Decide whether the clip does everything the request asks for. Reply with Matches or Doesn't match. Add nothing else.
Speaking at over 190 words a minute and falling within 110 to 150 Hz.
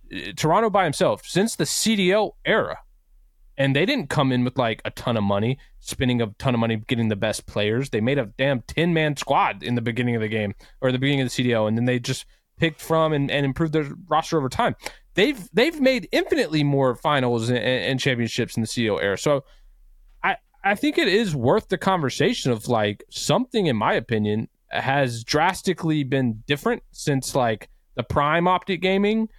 Matches